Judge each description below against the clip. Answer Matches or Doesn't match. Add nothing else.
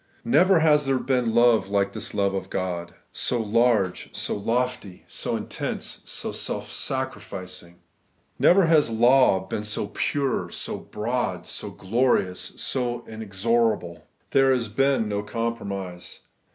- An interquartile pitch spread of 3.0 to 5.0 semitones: Matches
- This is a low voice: Matches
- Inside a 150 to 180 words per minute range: Doesn't match